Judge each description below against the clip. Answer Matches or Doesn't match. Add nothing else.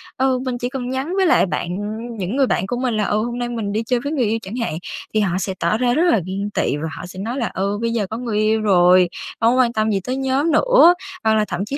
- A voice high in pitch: Matches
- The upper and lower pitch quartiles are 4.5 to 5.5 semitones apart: Doesn't match